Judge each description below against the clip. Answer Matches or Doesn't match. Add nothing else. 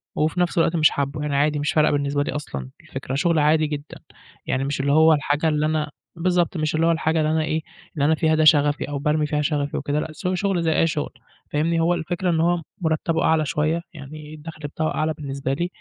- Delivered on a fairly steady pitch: Matches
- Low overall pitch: Doesn't match